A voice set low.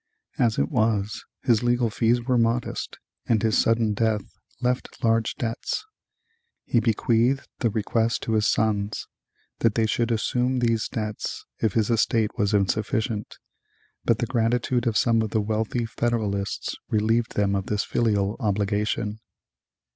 Yes: low, 110 Hz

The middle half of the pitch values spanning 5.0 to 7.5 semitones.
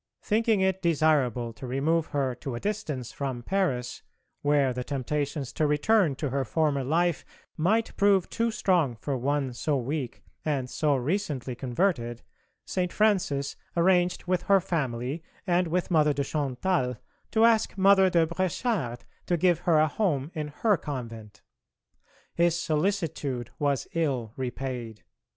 Yes: wide, 5.6 semitones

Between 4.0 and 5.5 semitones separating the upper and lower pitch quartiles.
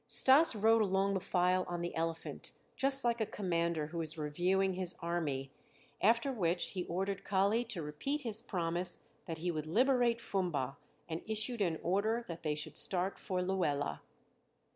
Yes: average, 4.6 semitones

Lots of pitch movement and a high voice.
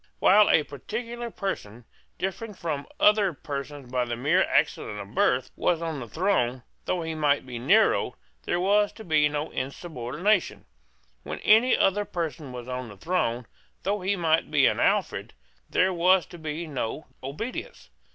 No: wide, 6.8 semitones; medium, 160 Hz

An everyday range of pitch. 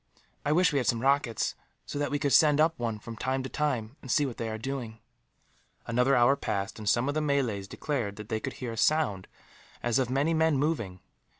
Yes: average, 4.2 semitones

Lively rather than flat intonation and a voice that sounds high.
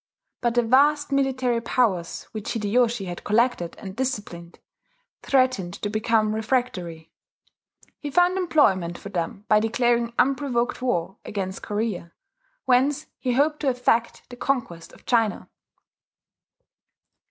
No: average, 4.5 semitones; high, 235 Hz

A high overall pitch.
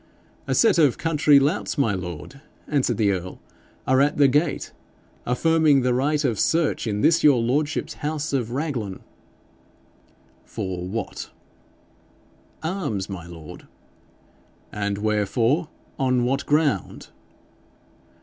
No: low, 130 Hz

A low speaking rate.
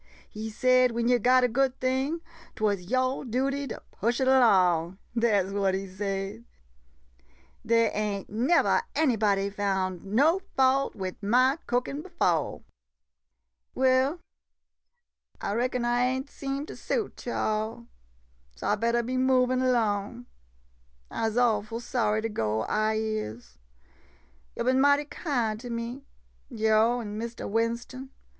No: average, 150 wpm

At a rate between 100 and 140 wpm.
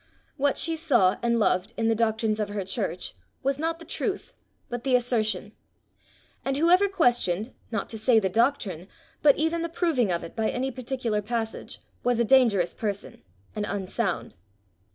No: average, 170 wpm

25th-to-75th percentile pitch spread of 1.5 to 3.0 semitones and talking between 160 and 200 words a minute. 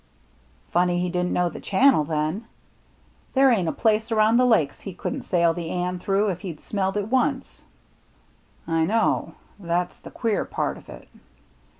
No: average, 4.4 semitones; average, 180 wpm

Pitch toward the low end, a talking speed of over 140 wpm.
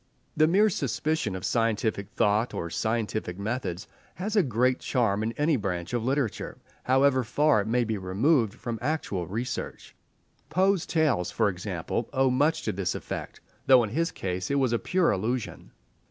Yes: low, 120 Hz; average, 170 wpm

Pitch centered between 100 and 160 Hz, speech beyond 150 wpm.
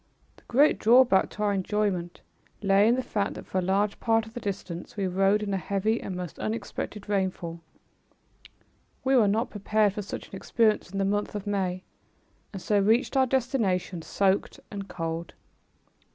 No: high, 200 Hz; average, 180 wpm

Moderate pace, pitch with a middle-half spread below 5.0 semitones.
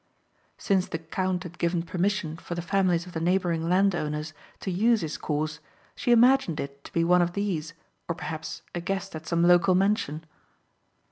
Yes: average, 180 wpm; average, 2.9 semitones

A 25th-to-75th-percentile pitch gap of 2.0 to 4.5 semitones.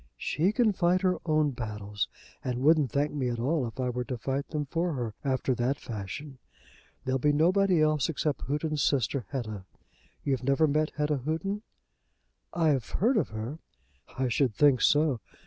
Yes: average, 3.9 semitones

